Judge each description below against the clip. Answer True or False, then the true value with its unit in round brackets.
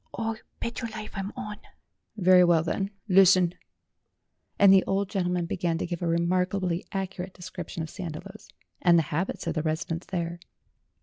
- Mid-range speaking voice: True (180 Hz)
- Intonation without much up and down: True (2.3 semitones)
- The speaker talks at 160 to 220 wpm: True (165 wpm)